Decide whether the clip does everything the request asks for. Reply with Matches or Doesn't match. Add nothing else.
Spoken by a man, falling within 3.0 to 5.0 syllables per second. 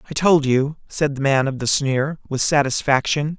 Matches